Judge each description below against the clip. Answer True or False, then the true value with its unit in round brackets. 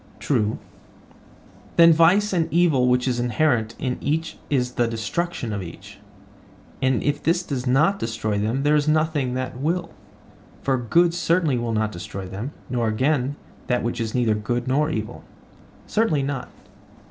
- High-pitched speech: False (130 Hz)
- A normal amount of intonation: True (5.0 semitones)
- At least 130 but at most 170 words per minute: True (160 wpm)